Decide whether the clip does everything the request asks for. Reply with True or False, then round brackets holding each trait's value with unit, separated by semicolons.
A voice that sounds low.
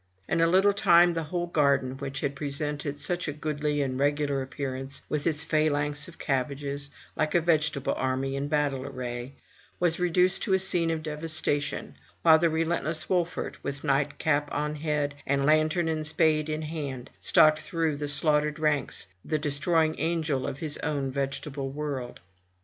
False (150 Hz)